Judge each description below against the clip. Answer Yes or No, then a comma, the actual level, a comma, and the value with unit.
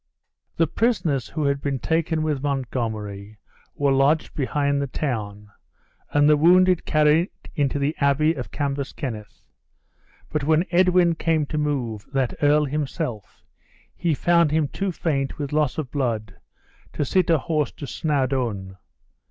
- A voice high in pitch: No, medium, 145 Hz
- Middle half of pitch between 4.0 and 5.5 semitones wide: No, average, 3.2 semitones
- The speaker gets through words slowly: No, average, 145 wpm